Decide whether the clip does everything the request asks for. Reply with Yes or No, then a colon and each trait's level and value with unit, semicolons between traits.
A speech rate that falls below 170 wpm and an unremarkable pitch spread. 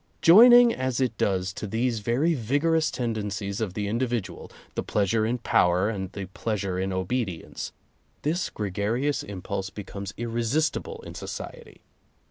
Yes: average, 150 wpm; average, 4.9 semitones